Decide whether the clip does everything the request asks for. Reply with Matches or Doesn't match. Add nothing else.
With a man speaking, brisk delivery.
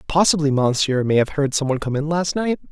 Matches